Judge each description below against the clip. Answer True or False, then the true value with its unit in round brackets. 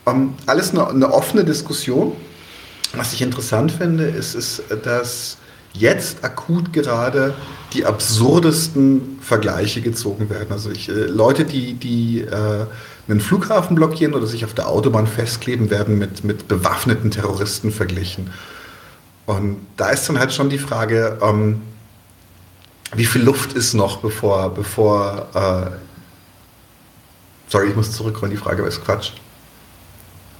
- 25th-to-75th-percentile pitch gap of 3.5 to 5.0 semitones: True (4.0 semitones)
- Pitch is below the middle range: True (110 Hz)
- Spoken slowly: False (135 wpm)